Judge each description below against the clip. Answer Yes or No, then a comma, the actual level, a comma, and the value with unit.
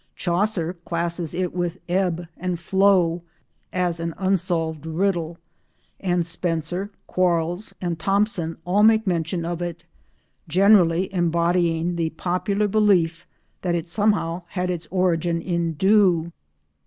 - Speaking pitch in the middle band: Yes, medium, 175 Hz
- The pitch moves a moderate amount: No, narrow, 2.1 semitones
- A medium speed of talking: No, slow, 120 wpm